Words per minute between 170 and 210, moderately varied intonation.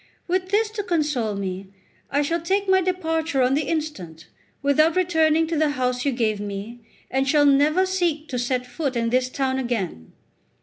Yes: average, 185 wpm; average, 5.0 semitones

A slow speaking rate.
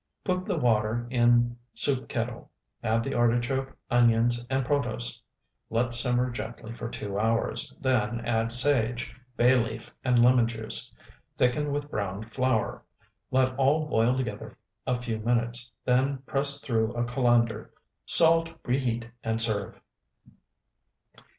Yes: slow, 130 wpm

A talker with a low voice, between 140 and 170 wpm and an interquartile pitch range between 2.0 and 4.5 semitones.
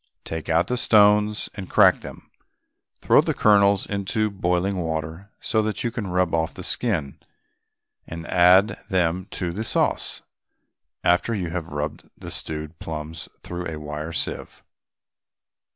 Yes: very low, 90 Hz; average, 145 wpm; average, 4.0 semitones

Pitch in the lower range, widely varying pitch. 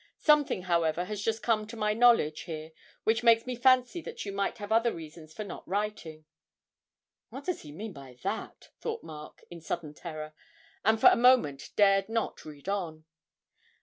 No: high, 200 Hz; wide, 6.2 semitones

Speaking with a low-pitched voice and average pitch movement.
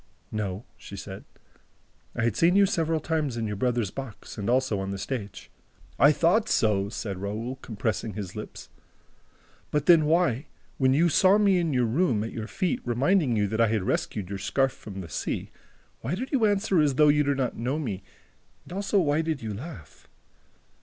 No: low, 130 Hz; wide, 7.1 semitones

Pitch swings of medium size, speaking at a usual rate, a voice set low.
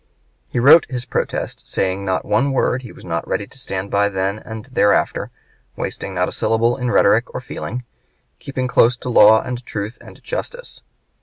Yes: average, 4.0 semitones; average, 180 wpm; low, 115 Hz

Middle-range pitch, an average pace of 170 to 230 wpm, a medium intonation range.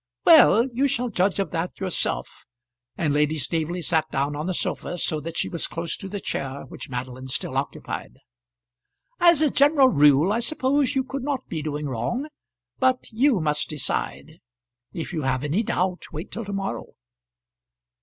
No: medium, 175 Hz; average, 175 wpm; wide, 8.6 semitones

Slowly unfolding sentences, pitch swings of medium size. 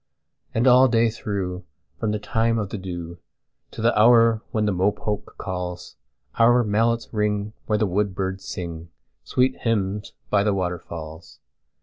Yes: slow, 130 wpm; average, 3.8 semitones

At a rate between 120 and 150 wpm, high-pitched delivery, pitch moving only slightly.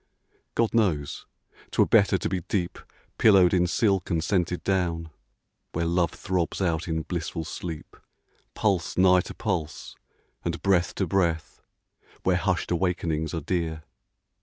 No: average, 140 wpm; very low, 90 Hz; narrow, 2.3 semitones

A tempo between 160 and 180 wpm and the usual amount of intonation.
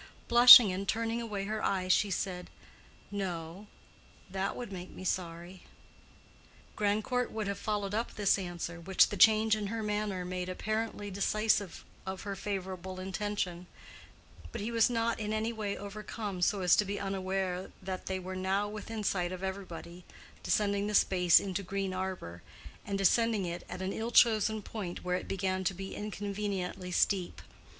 No: average, 165 wpm; narrow, 2.3 semitones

